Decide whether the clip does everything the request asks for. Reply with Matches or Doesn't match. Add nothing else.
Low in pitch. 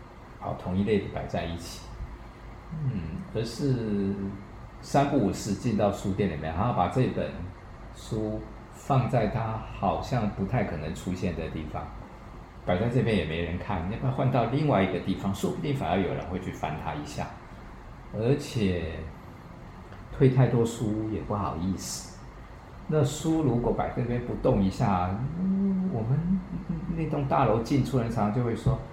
Matches